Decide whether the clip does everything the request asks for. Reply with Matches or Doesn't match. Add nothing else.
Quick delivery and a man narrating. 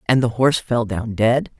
Doesn't match